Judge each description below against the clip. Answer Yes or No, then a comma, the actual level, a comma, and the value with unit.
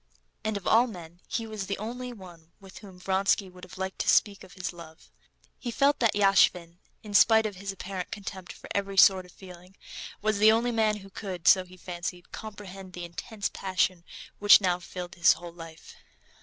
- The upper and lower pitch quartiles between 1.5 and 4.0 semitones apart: Yes, average, 2.7 semitones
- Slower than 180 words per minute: No, average, 195 wpm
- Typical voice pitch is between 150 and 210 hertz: Yes, high, 190 Hz